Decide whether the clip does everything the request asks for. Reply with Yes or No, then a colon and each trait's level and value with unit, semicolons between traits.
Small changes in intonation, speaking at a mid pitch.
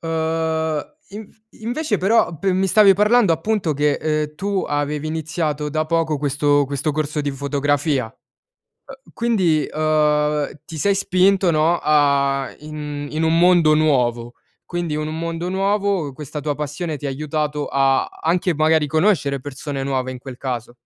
No: average, 3.2 semitones; medium, 155 Hz